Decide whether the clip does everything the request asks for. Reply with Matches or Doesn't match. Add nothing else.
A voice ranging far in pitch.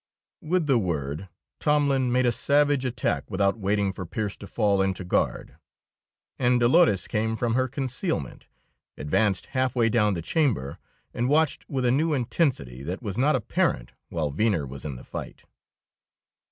Matches